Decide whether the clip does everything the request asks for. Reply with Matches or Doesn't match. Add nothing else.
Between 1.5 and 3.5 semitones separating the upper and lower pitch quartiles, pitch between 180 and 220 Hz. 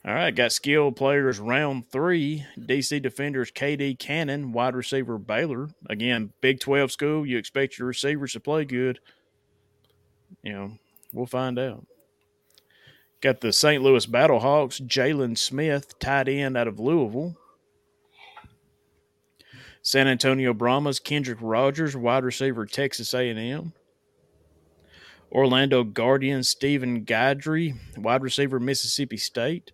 Doesn't match